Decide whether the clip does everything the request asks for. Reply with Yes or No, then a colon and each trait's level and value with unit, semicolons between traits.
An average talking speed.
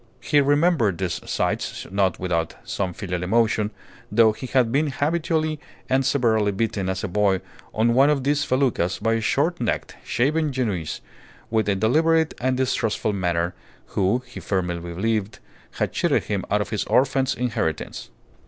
Yes: average, 160 wpm